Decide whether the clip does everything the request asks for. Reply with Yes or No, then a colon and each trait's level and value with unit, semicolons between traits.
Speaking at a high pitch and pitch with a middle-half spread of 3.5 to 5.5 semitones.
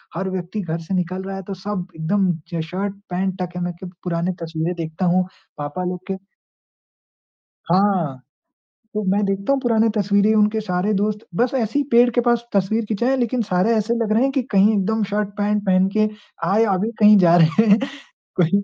No: high, 195 Hz; average, 3.1 semitones